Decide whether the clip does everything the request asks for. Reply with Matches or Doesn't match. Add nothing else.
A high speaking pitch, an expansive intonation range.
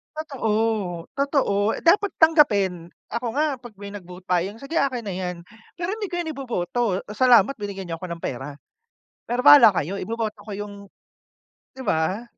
Matches